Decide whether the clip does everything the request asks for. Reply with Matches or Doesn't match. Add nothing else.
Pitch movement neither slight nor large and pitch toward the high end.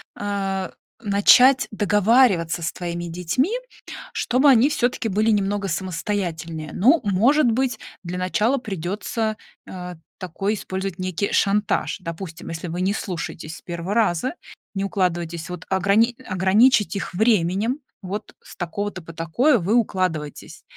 Matches